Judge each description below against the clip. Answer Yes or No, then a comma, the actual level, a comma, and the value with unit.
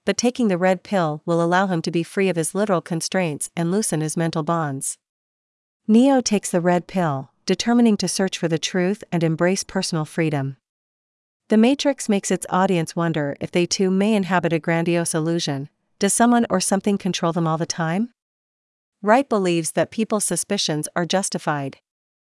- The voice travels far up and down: No, average, 3.3 semitones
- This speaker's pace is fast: No, average, 175 wpm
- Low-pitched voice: No, medium, 180 Hz